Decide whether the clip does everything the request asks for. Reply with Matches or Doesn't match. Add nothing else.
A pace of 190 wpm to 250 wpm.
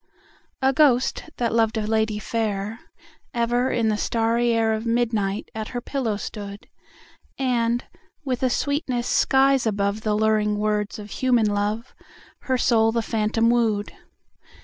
Doesn't match